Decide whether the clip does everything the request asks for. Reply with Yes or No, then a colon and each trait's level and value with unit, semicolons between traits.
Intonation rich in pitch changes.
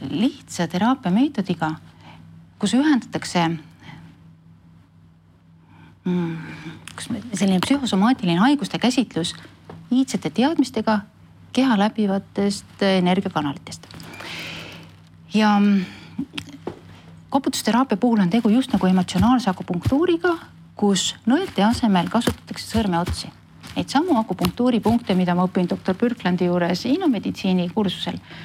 Yes: wide, 5.8 semitones